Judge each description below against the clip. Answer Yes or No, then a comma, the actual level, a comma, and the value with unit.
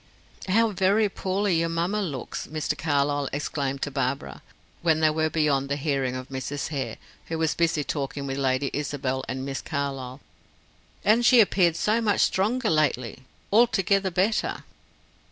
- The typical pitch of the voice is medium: Yes, medium, 155 Hz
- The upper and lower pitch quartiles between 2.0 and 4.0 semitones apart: No, wide, 5.6 semitones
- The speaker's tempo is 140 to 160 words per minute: Yes, average, 155 wpm